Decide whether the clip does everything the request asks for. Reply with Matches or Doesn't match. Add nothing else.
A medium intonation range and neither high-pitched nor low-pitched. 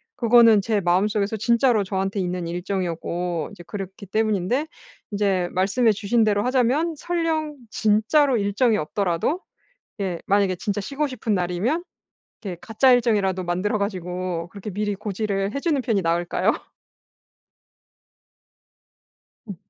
Doesn't match